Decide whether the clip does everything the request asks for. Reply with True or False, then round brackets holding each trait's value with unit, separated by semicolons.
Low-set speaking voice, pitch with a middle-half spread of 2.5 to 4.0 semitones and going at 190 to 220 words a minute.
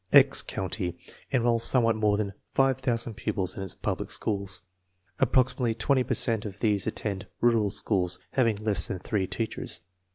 False (110 Hz; 3.2 semitones; 165 wpm)